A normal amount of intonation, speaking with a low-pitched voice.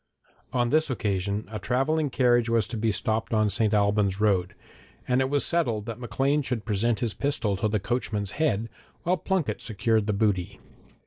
Yes: average, 3.7 semitones; low, 110 Hz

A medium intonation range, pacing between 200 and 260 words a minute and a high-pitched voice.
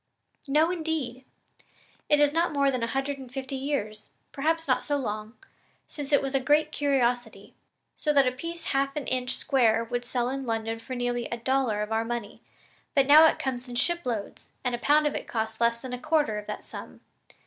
Yes: average, 3.4 semitones; fast, 205 wpm; very high, 260 Hz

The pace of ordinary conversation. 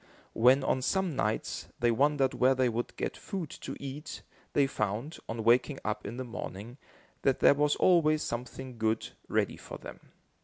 Yes: average, 170 wpm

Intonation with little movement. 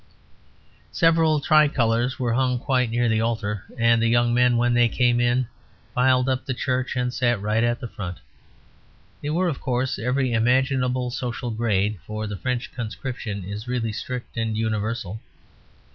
Yes: narrow, 2.2 semitones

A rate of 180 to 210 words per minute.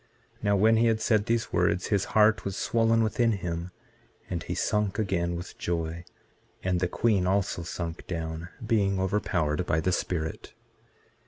No: average, 160 wpm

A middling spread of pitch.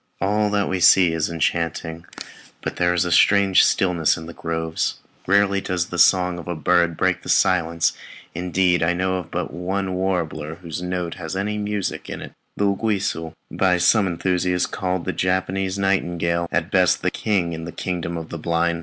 No: narrow, 2.0 semitones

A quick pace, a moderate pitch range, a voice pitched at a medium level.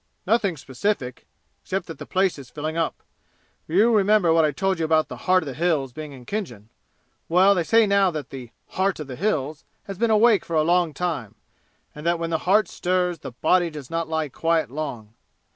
Yes: fast, 210 wpm; average, 4.2 semitones; medium, 165 Hz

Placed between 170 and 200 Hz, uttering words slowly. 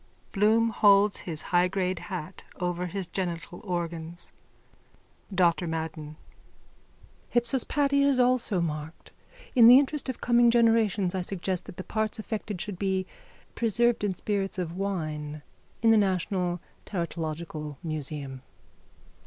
Yes: medium, 185 Hz; slow, 130 wpm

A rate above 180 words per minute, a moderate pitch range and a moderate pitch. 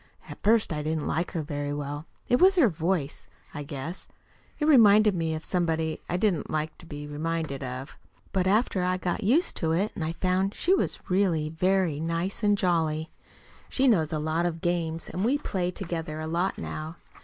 Yes: average, 190 wpm; average, 3.6 semitones; medium, 170 Hz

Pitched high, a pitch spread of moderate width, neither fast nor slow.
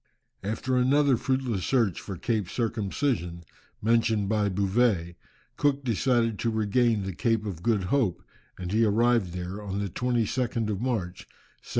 No: low, 110 Hz; average, 3.9 semitones; average, 145 wpm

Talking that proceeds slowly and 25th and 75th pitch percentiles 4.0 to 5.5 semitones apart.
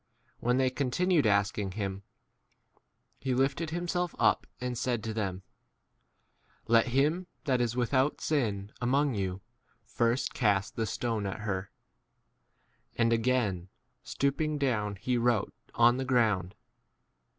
Yes: slow, 130 wpm; average, 4.3 semitones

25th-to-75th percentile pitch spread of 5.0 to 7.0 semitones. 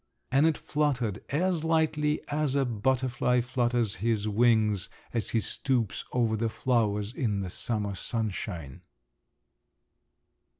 No: average, 4.2 semitones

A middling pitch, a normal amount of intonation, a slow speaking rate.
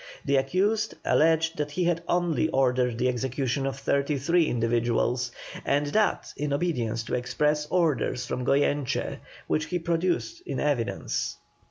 No: medium, 145 Hz; average, 4.6 semitones; average, 145 wpm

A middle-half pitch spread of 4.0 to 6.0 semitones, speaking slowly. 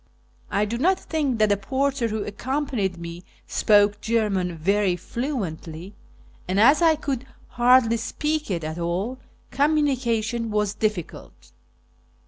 Yes: wide, 5.4 semitones; slow, 125 wpm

